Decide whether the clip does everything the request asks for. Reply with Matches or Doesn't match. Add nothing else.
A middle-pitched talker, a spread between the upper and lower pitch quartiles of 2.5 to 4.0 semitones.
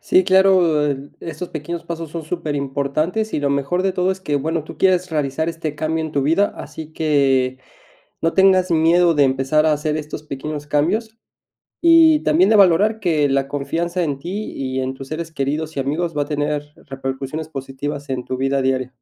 Matches